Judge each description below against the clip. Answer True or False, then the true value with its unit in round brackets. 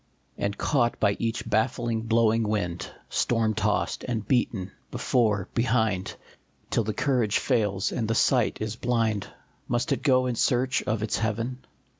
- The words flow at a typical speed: True (150 wpm)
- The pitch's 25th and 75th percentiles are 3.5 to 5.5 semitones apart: False (2.4 semitones)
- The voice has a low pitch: True (115 Hz)